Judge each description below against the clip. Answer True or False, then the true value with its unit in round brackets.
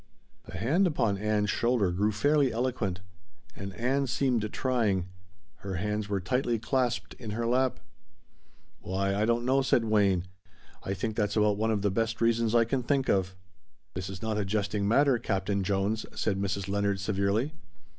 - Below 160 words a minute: False (175 wpm)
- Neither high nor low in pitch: False (105 Hz)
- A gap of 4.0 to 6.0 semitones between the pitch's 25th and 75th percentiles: False (3.4 semitones)